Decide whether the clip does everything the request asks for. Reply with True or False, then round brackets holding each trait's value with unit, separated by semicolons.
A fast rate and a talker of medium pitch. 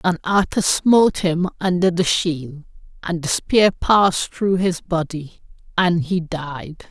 False (150 wpm; 175 Hz)